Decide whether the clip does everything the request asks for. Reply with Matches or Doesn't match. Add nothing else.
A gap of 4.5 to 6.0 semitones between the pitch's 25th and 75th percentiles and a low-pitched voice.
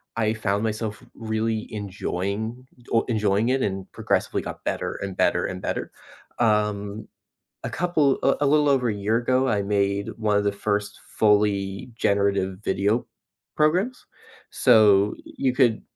Doesn't match